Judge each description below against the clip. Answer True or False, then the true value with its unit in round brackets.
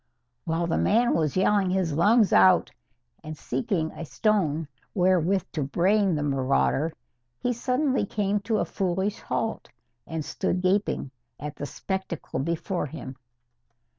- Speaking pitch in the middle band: True (180 Hz)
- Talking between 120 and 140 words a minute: True (135 wpm)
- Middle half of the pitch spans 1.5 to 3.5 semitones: False (4.8 semitones)